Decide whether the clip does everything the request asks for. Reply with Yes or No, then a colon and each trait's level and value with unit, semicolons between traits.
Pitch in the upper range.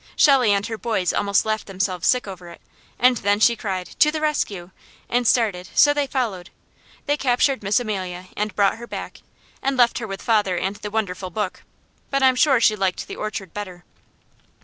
Yes: high, 210 Hz